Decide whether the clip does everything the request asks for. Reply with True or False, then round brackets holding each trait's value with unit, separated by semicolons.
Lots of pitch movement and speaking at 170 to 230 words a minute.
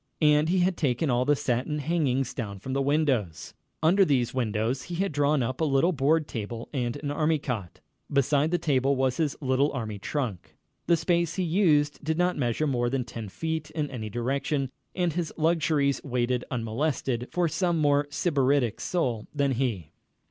False (4.3 semitones; 180 wpm)